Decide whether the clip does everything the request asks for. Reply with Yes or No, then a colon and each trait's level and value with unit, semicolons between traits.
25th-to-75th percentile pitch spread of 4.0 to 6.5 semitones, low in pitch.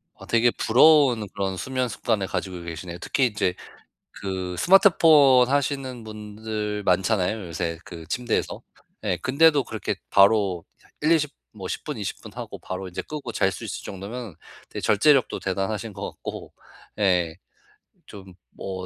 Yes: average, 5.3 semitones; low, 105 Hz